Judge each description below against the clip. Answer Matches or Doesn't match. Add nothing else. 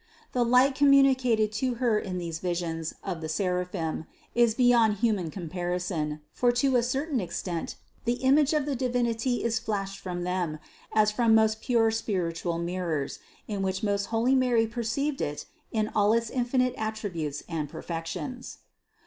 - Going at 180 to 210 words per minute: Doesn't match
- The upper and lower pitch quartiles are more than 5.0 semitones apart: Matches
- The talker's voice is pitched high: Matches